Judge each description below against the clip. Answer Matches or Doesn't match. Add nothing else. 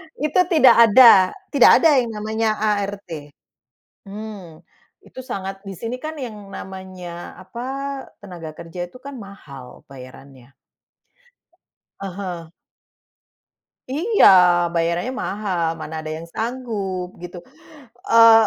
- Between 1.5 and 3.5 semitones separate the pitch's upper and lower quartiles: Doesn't match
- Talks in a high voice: Matches